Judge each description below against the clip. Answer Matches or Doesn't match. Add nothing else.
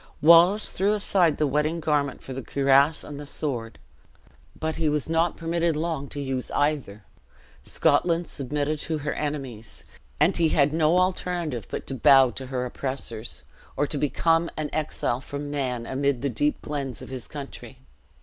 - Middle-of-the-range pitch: Matches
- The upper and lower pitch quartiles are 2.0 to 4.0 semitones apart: Matches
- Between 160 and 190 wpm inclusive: Matches